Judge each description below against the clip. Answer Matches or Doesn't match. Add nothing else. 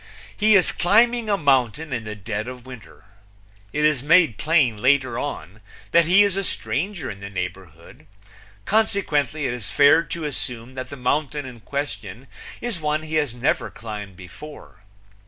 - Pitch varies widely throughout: Matches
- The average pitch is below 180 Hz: Matches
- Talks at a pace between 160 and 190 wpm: Matches